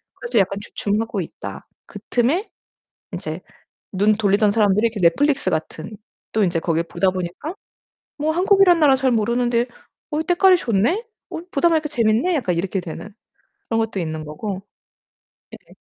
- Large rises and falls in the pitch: Yes, wide, 7.6 semitones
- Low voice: No, high, 225 Hz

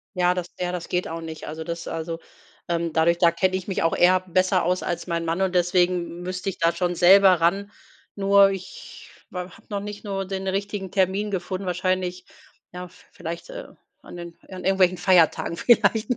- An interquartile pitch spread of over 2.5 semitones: No, narrow, 2.0 semitones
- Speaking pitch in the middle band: Yes, medium, 180 Hz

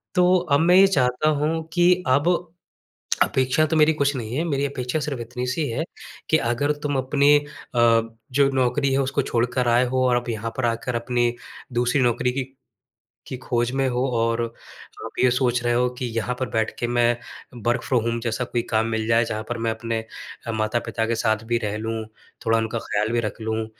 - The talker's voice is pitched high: No, low, 120 Hz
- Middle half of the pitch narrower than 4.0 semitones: Yes, average, 3.0 semitones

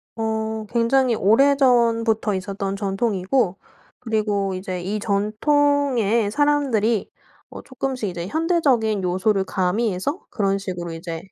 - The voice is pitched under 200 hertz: No, high, 215 Hz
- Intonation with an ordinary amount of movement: Yes, average, 4.1 semitones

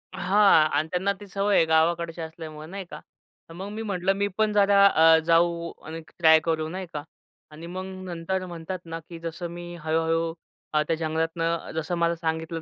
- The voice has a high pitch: No, medium, 170 Hz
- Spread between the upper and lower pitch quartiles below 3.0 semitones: Yes, narrow, 2.4 semitones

